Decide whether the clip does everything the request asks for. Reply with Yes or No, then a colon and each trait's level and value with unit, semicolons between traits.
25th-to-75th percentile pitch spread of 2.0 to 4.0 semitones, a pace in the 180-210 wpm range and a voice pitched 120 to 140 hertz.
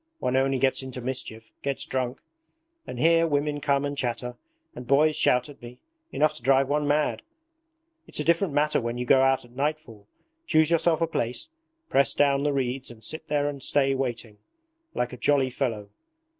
Yes: average, 2.9 semitones; average, 185 wpm; low, 135 Hz